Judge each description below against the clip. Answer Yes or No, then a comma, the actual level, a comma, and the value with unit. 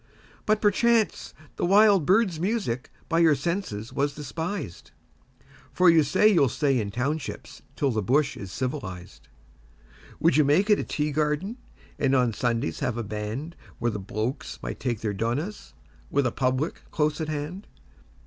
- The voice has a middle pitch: Yes, medium, 145 Hz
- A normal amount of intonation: No, wide, 6.3 semitones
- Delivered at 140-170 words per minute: Yes, average, 160 wpm